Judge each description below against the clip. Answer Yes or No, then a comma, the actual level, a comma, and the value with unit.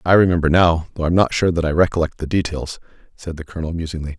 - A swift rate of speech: Yes, fast, 230 wpm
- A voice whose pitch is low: Yes, very low, 80 Hz